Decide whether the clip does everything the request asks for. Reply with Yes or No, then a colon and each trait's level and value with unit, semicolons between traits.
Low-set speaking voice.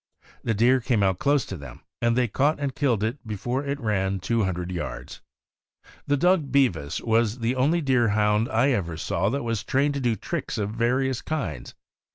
Yes: low, 115 Hz